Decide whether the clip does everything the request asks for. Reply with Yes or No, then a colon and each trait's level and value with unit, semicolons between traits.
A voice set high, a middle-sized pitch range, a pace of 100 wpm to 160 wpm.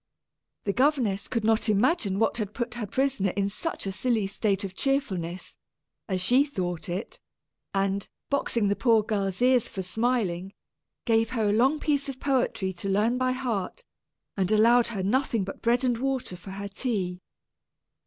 No: high, 220 Hz; average, 4.4 semitones; average, 170 wpm